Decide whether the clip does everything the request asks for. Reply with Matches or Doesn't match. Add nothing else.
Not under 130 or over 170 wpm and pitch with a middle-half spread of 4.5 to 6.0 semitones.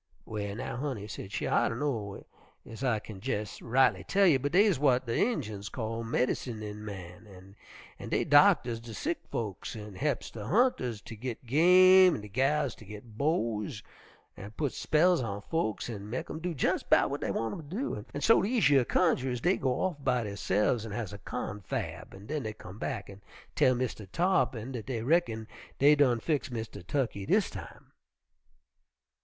Doesn't match